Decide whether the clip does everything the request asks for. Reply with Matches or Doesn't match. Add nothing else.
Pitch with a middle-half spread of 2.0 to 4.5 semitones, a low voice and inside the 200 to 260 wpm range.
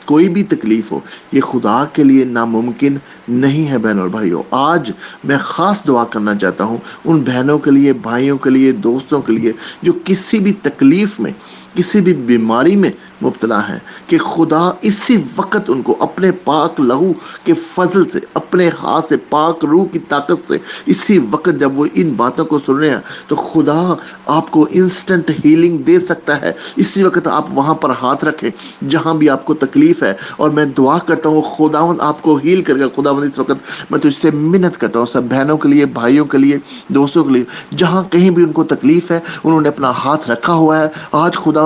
Doesn't match